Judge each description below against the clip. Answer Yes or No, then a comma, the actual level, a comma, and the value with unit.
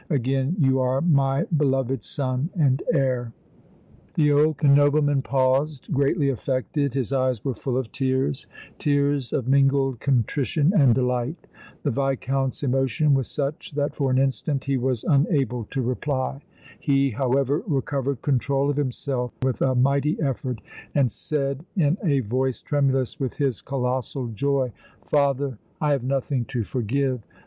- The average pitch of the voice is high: No, low, 135 Hz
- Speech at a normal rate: Yes, average, 145 wpm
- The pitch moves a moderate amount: No, narrow, 1.7 semitones